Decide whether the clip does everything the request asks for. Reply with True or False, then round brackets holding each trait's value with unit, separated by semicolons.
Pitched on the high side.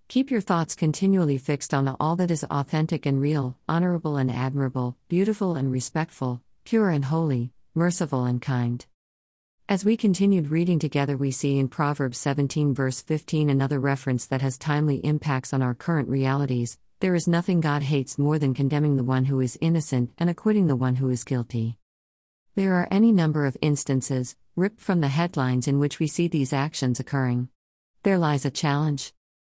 False (140 Hz)